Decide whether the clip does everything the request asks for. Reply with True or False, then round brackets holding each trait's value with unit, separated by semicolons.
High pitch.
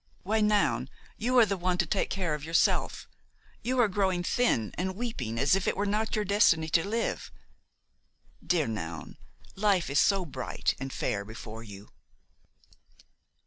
False (180 Hz)